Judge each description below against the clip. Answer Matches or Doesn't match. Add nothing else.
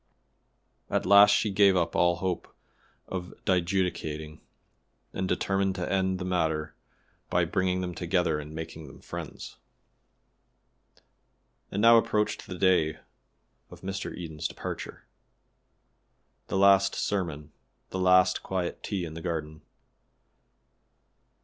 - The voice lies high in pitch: Doesn't match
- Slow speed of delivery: Matches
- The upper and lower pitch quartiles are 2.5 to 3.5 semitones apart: Matches